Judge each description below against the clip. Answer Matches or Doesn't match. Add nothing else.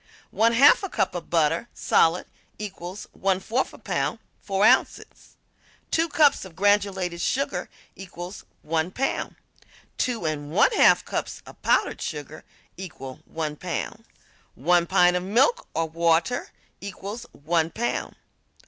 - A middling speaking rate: Doesn't match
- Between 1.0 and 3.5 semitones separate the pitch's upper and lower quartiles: Doesn't match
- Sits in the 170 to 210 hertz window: Matches